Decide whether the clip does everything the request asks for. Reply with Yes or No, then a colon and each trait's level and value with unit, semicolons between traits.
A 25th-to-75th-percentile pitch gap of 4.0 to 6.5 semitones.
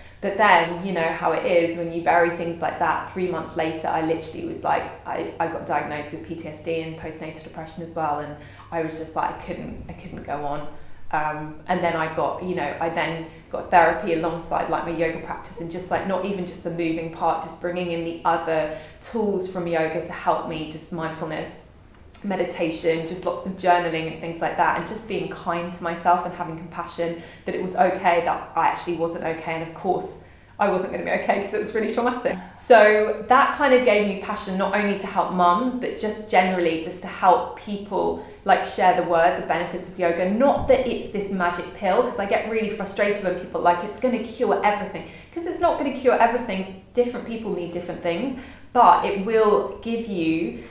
No: average, 3.3 semitones